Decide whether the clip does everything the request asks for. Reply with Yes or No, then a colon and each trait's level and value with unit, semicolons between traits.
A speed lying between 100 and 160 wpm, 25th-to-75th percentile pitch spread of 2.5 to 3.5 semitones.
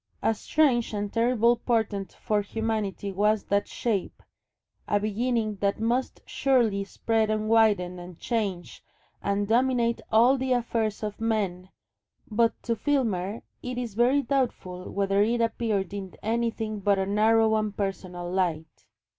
Yes: average, 140 wpm; average, 2.8 semitones